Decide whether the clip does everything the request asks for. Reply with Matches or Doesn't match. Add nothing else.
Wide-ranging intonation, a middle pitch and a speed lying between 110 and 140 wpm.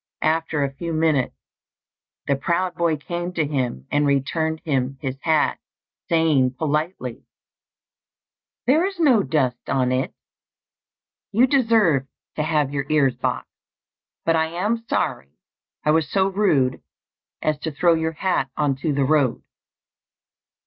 Doesn't match